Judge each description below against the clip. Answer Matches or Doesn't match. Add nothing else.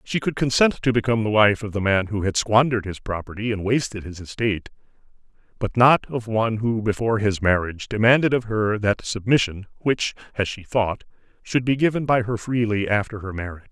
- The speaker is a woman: Doesn't match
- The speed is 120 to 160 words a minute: Doesn't match